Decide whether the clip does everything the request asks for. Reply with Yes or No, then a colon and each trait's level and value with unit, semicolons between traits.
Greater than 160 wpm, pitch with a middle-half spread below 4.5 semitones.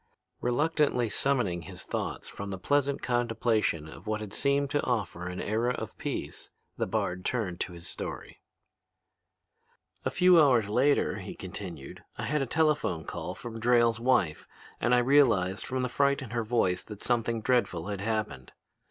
No: average, 170 wpm; average, 5.2 semitones